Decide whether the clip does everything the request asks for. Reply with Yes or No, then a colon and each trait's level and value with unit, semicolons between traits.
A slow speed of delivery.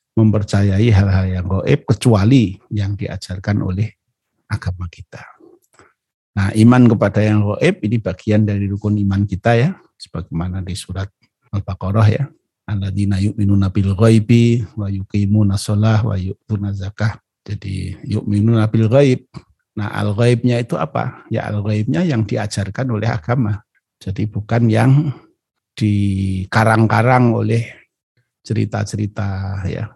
No: average, 110 wpm